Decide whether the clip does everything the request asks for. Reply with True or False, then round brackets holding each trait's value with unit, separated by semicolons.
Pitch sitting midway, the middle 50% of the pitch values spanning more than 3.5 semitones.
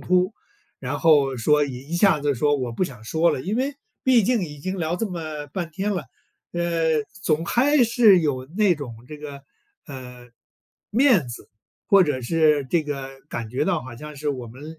True (150 Hz; 5.1 semitones)